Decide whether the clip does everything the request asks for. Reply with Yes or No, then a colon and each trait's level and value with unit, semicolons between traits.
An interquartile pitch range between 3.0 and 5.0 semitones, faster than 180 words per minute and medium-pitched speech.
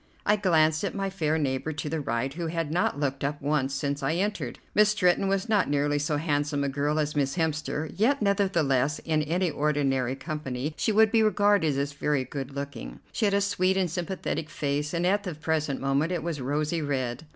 Yes: average, 4.2 semitones; fast, 205 wpm; medium, 155 Hz